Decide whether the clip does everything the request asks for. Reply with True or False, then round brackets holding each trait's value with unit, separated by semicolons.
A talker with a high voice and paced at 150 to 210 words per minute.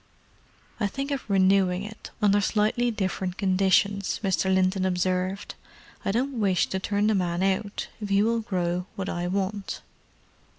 True (195 Hz; 155 wpm)